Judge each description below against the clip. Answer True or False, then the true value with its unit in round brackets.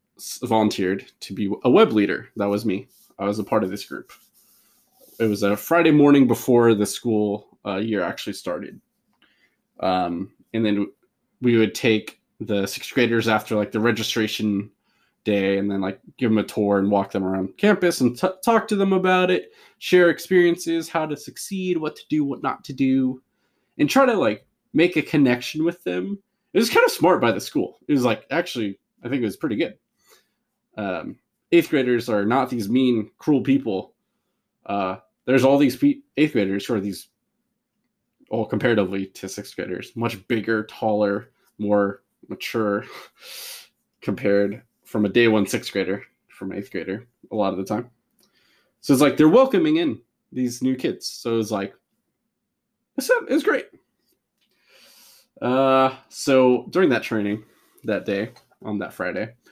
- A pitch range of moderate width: False (6.7 semitones)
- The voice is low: True (120 Hz)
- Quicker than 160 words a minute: True (170 wpm)